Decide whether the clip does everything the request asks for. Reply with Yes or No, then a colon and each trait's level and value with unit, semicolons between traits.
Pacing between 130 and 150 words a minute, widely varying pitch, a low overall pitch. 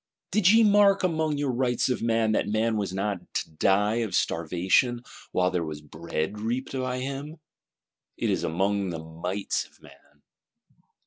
No: average, 165 wpm; wide, 6.4 semitones; low, 110 Hz